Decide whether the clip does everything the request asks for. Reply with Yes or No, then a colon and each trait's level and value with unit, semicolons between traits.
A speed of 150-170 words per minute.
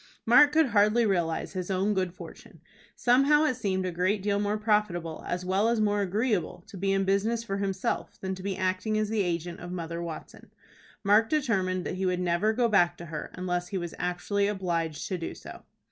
No: fast, 205 wpm